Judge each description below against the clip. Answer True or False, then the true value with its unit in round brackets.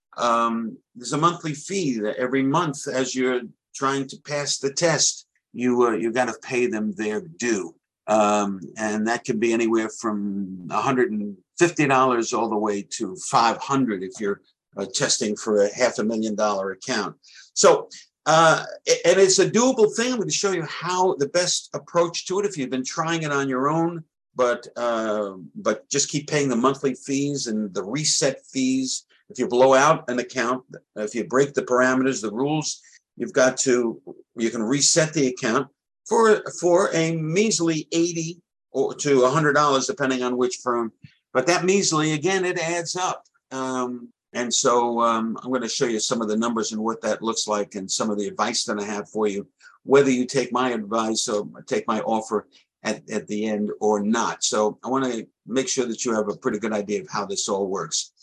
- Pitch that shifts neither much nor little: False (5.8 semitones)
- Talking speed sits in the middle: True (195 wpm)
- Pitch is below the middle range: True (125 Hz)